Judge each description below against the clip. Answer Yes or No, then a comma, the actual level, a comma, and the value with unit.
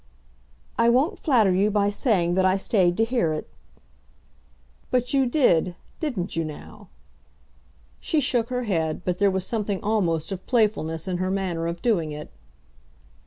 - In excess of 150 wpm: Yes, average, 160 wpm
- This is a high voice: Yes, high, 195 Hz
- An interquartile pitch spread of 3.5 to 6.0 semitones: Yes, average, 5.1 semitones